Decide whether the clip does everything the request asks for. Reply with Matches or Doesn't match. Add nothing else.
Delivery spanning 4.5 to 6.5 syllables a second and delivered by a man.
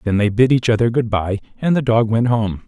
Matches